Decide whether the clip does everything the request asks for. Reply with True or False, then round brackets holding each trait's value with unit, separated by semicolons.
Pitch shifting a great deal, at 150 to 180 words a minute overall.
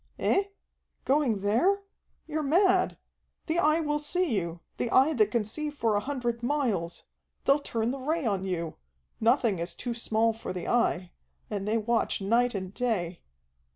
True (6.4 semitones; 165 wpm)